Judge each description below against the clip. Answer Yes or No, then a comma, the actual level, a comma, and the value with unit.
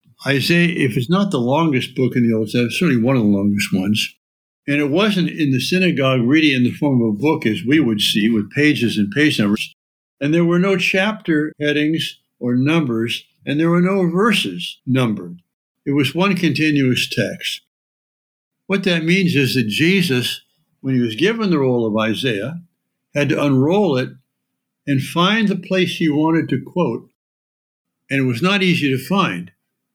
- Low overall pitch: No, medium, 145 Hz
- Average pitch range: No, wide, 6.0 semitones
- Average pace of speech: Yes, average, 185 wpm